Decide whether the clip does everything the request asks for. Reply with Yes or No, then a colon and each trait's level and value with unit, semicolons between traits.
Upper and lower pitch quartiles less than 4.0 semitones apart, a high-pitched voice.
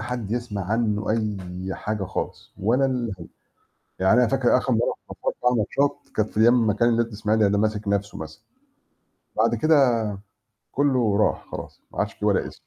No: average, 3.2 semitones; low, 110 Hz